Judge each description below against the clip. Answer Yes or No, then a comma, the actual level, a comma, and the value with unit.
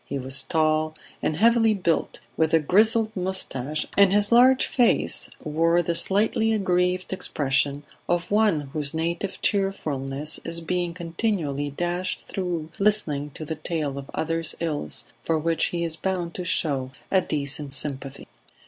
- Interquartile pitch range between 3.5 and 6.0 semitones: Yes, average, 4.2 semitones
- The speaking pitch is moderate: Yes, medium, 165 Hz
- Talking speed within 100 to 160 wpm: Yes, average, 150 wpm